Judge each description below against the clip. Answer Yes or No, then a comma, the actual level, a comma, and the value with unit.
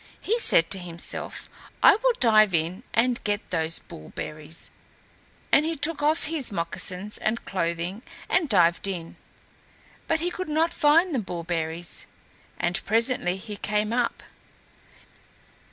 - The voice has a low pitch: No, high, 210 Hz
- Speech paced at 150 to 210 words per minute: No, slow, 135 wpm